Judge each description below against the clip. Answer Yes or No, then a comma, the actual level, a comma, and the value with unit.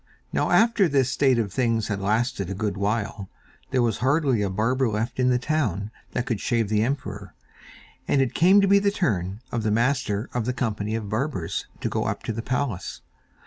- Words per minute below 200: No, fast, 205 wpm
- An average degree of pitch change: Yes, average, 4.1 semitones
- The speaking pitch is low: Yes, low, 115 Hz